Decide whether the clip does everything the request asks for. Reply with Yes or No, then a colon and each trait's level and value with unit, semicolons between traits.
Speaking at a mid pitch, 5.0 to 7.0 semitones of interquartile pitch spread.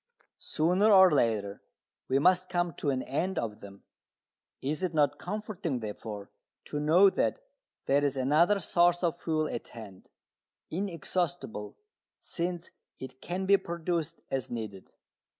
Yes: medium, 160 Hz; wide, 5.5 semitones